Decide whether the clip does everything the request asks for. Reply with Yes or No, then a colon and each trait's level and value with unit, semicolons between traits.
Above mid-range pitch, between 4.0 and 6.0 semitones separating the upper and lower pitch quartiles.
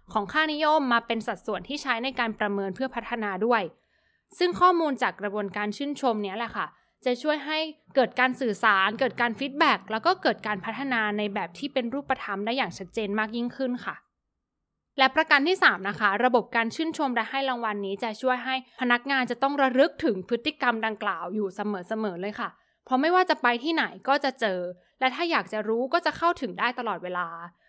Yes: high, 240 Hz; average, 4.6 semitones